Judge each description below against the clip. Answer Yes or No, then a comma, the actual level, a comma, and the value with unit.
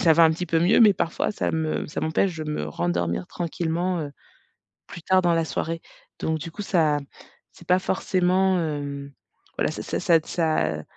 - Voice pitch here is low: No, medium, 165 Hz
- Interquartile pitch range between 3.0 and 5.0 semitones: No, narrow, 2.6 semitones